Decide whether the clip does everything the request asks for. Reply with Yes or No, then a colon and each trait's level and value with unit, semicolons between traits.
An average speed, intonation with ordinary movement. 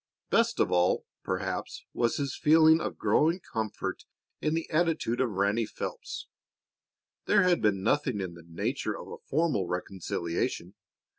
No: average, 145 wpm; wide, 9.0 semitones